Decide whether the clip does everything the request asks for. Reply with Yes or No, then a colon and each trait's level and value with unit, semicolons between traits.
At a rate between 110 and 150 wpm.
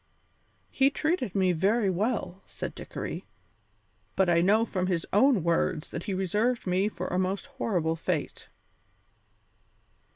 Yes: slow, 135 wpm